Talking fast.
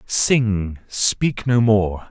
No: slow, 115 wpm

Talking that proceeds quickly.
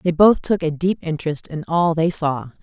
Yes: fast, 230 wpm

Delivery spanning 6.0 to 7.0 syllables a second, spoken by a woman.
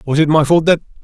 No: 6.9 syllables/s; male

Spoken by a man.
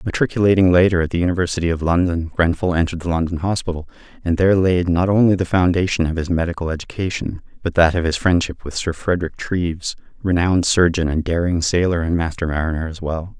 Yes: male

